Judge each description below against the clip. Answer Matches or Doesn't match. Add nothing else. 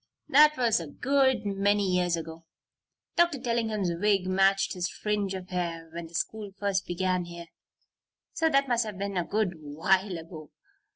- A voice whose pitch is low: Doesn't match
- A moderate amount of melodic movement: Matches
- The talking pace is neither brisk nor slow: Matches